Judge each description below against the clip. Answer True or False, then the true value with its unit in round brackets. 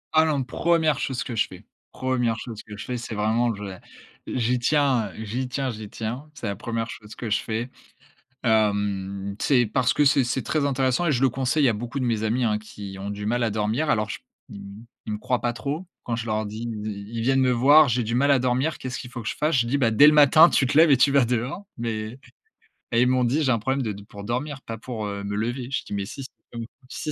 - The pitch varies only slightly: False (3.6 semitones)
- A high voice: False (120 Hz)